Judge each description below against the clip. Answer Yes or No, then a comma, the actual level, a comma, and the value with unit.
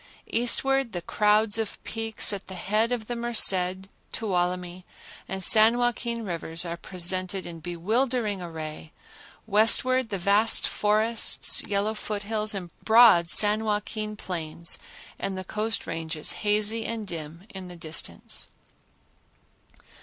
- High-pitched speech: Yes, high, 205 Hz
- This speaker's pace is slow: Yes, slow, 130 wpm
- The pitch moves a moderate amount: Yes, average, 3.8 semitones